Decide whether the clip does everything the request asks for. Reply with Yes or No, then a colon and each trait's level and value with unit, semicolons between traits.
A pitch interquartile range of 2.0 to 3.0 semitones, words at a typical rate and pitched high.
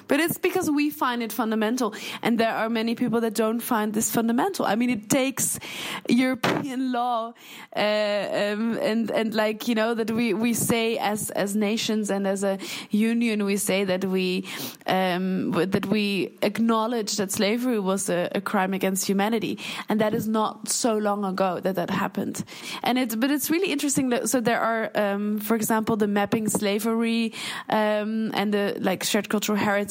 Yes: narrow, 2.4 semitones; average, 180 wpm; high, 220 Hz